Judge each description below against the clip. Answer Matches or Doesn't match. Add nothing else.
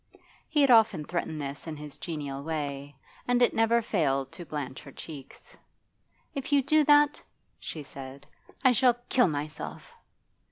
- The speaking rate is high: Doesn't match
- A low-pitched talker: Doesn't match